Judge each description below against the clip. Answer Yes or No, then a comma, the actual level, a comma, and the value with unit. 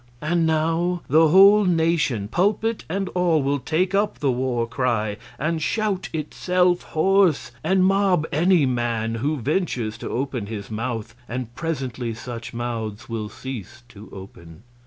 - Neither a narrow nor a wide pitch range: No, wide, 7.2 semitones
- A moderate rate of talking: Yes, average, 150 wpm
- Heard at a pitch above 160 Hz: No, medium, 140 Hz